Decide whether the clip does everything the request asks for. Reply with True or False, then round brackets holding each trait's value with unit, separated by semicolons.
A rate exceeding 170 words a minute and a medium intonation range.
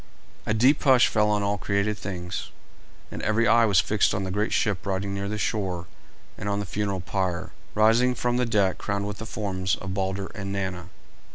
False (200 wpm; 2.1 semitones)